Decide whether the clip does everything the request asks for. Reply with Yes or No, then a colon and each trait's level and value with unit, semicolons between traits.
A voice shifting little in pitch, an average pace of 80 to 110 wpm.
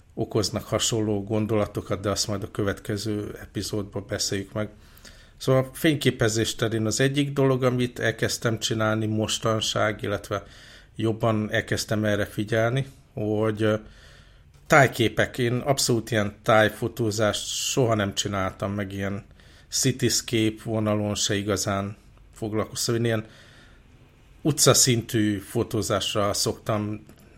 Yes: narrow, 2.1 semitones; slow, 105 wpm